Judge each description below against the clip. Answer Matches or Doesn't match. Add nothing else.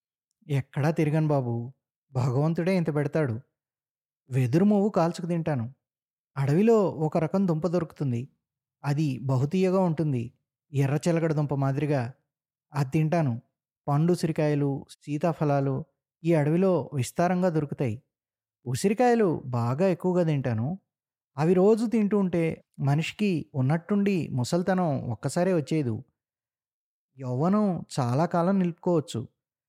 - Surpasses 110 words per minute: Doesn't match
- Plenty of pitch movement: Doesn't match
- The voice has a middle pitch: Matches